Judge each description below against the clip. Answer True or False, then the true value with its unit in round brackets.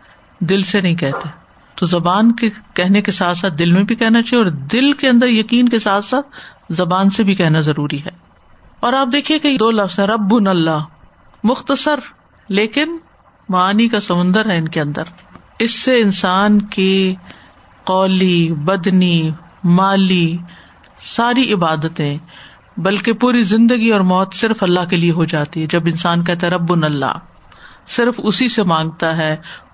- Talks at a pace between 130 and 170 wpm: True (160 wpm)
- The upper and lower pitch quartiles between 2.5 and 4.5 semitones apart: False (4.9 semitones)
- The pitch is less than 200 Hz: True (190 Hz)